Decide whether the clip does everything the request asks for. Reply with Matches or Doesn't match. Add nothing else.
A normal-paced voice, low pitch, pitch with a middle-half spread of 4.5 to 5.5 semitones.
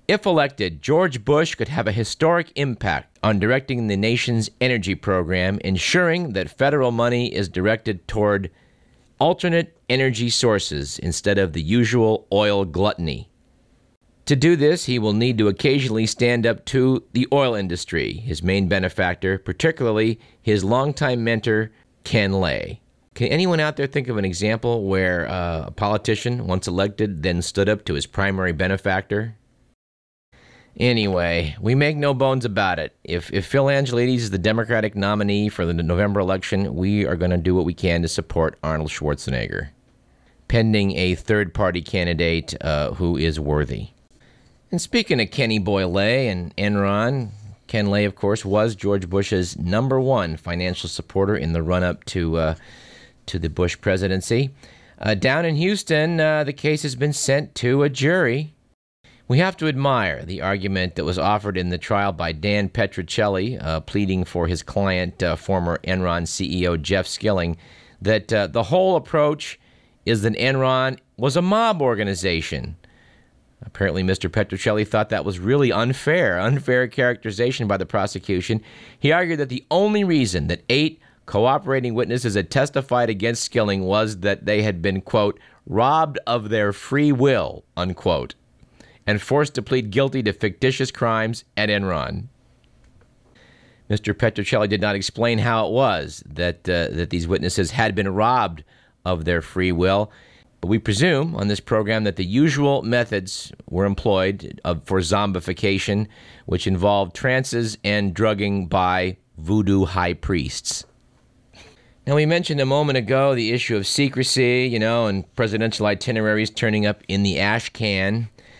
Matches